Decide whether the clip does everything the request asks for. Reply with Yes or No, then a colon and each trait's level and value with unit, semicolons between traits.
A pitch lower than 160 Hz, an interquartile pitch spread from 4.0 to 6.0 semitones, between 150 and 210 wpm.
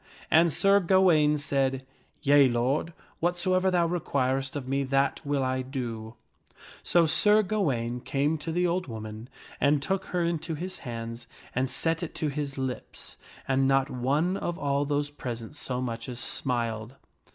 Yes: medium, 140 Hz; average, 4.6 semitones; average, 160 wpm